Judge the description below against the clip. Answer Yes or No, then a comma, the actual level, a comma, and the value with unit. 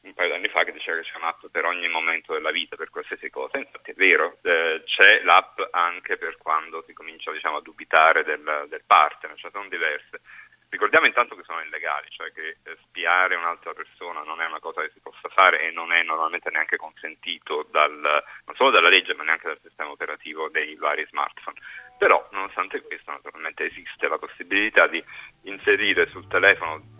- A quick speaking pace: Yes, fast, 195 wpm